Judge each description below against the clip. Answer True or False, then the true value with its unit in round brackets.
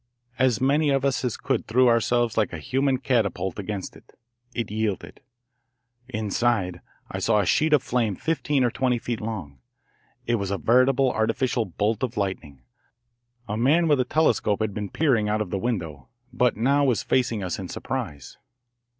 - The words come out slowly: False (175 wpm)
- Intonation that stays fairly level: False (4.1 semitones)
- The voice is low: True (115 Hz)